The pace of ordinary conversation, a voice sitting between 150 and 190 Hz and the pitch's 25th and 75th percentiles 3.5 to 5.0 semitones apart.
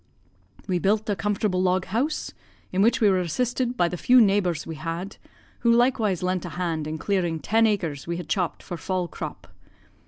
Yes: average, 190 wpm; medium, 185 Hz; average, 4.0 semitones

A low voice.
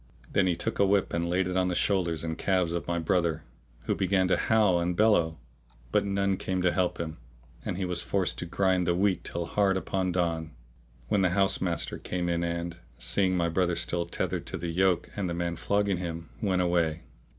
Yes: very low, 90 Hz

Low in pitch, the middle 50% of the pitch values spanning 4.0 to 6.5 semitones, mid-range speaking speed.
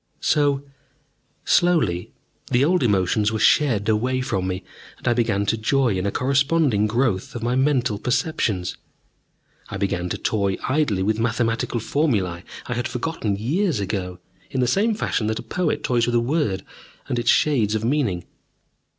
Yes: low, 120 Hz; average, 5.1 semitones; average, 165 wpm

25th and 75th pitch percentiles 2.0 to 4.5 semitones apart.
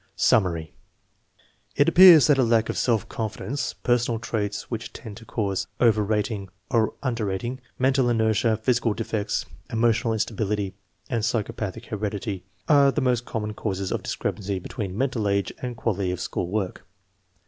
Yes: average, 2.8 semitones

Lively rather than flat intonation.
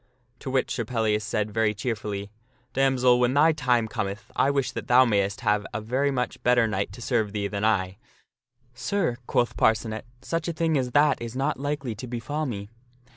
No: average, 3.8 semitones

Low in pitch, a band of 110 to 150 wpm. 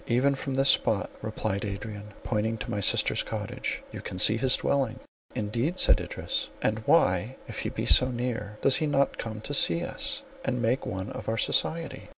No: low, 115 Hz; average, 190 wpm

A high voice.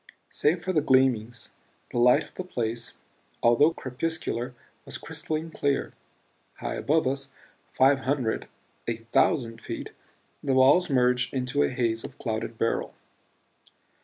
No: low, 130 Hz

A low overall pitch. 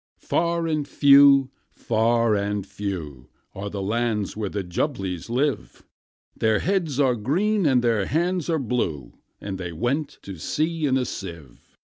Yes: low, 120 Hz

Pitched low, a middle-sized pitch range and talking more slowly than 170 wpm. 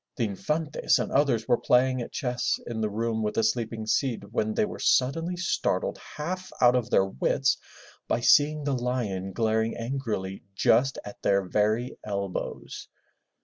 Yes: low, 120 Hz; average, 3.7 semitones; average, 160 wpm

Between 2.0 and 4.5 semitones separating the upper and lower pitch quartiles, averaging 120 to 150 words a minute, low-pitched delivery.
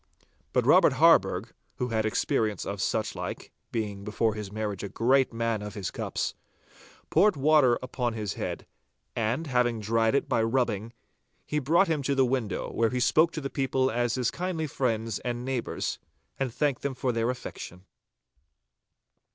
No: average, 3.5 semitones; average, 165 wpm; low, 120 Hz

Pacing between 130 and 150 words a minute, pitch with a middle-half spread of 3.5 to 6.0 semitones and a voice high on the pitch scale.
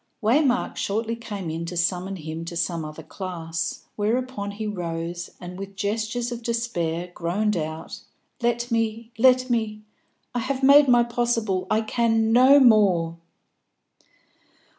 Yes: average, 140 wpm; average, 5.2 semitones; high, 215 Hz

